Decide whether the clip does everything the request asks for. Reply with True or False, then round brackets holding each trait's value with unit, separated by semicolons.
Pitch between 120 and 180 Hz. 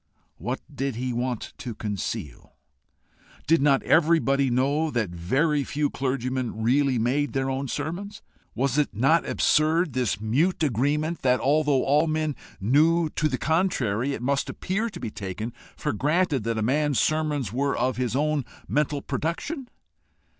True (140 Hz)